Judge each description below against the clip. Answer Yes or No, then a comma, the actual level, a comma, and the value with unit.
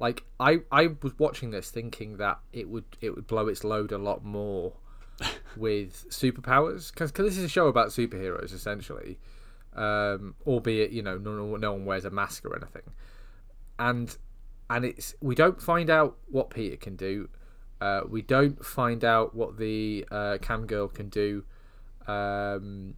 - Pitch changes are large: No, average, 3.3 semitones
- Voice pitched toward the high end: No, low, 110 Hz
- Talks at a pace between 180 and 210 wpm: No, average, 165 wpm